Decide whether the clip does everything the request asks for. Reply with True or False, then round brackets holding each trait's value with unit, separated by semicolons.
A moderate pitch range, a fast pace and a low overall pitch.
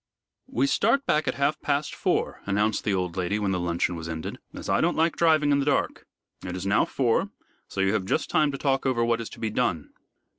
False (7.2 semitones; 235 wpm; 115 Hz)